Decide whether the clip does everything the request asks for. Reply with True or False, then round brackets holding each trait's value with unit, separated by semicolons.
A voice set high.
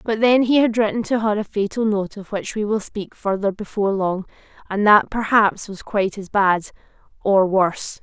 True (205 Hz)